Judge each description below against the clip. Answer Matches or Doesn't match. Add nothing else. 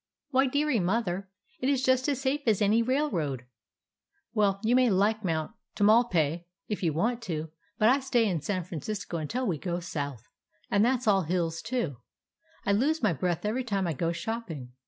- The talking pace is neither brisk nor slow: Matches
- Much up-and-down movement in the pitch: Matches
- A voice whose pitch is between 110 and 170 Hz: Doesn't match